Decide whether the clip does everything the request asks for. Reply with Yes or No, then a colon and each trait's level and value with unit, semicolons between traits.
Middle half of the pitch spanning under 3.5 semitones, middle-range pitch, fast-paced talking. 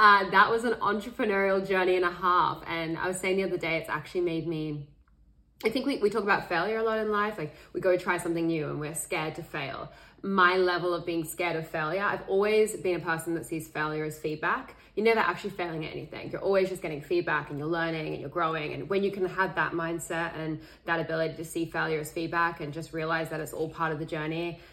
Yes: average, 2.9 semitones; medium, 170 Hz; fast, 245 wpm